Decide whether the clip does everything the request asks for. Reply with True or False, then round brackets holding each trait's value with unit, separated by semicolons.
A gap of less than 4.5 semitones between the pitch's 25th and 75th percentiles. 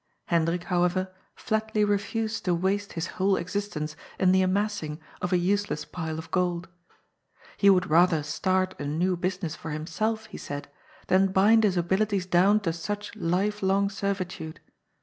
True (2.9 semitones)